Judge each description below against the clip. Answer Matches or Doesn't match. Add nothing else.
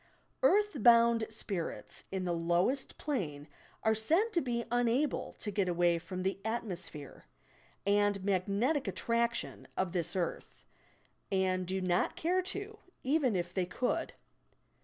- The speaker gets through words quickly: Doesn't match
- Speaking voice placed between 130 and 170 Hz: Doesn't match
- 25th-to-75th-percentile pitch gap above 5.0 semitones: Matches